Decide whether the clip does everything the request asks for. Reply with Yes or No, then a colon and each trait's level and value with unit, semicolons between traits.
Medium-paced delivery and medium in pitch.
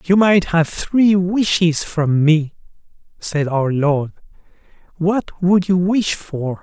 Yes: average, 145 wpm; medium, 175 Hz